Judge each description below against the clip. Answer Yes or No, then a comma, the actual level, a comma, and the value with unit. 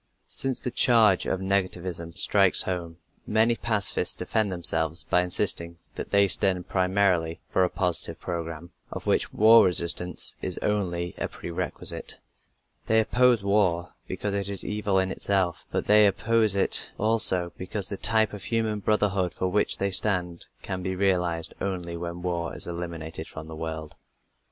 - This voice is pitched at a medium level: No, very low, 95 Hz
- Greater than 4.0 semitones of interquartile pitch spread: No, average, 3.2 semitones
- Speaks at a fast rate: No, average, 160 wpm